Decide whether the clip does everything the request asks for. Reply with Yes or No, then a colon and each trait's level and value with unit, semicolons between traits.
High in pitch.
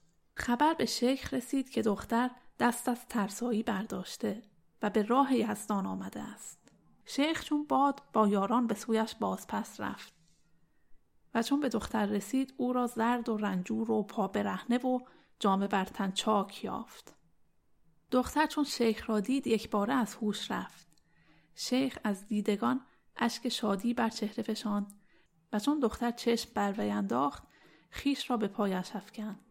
Yes: high, 225 Hz